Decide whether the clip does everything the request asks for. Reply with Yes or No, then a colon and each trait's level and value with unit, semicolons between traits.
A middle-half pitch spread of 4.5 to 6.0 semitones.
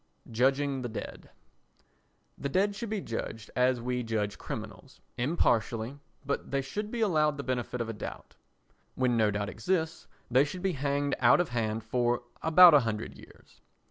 Yes: average, 5.0 semitones